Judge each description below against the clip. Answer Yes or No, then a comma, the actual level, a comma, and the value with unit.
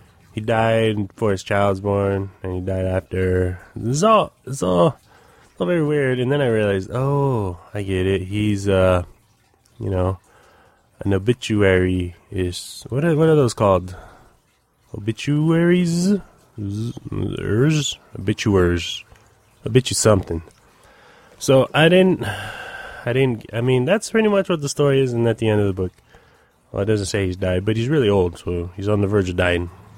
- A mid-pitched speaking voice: No, low, 105 Hz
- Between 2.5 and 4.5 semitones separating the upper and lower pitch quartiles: No, average, 5.2 semitones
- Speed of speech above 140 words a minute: Yes, average, 170 wpm